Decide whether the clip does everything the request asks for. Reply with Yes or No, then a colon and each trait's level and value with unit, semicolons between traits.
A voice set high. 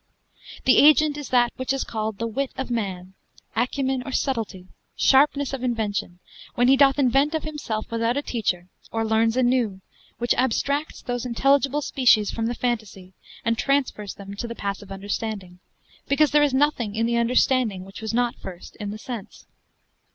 Yes: high, 235 Hz